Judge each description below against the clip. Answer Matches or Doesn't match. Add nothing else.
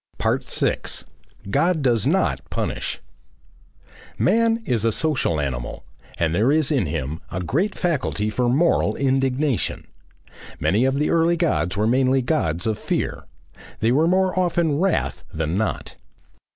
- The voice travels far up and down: Matches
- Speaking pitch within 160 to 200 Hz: Doesn't match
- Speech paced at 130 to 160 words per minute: Matches